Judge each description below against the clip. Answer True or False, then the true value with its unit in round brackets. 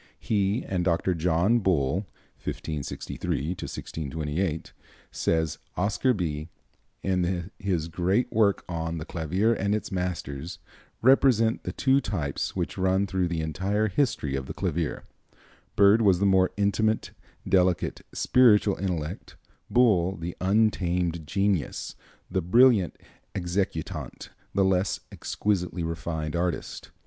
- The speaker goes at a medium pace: False (115 wpm)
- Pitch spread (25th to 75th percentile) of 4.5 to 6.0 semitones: False (3.5 semitones)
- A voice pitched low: True (90 Hz)